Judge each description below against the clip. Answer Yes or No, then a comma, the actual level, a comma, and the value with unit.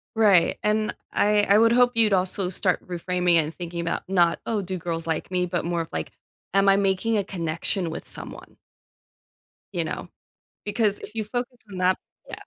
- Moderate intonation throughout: Yes, average, 3.4 semitones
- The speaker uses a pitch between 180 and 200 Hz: Yes, medium, 185 Hz